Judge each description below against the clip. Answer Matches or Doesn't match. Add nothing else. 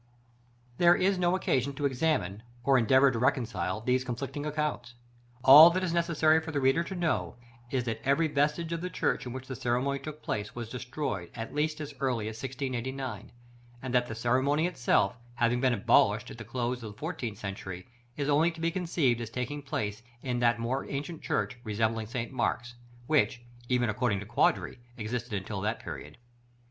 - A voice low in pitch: Matches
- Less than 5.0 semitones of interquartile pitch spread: Matches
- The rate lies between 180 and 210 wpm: Matches